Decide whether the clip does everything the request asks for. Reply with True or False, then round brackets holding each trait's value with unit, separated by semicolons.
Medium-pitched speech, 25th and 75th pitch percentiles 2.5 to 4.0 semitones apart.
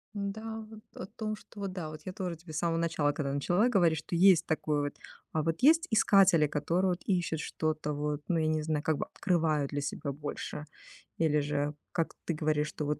True (160 Hz; 3.6 semitones)